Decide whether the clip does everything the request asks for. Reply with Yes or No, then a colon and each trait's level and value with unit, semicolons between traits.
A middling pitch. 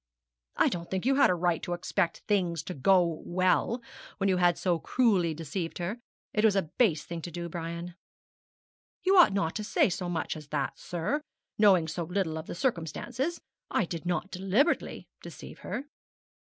Yes: medium, 180 Hz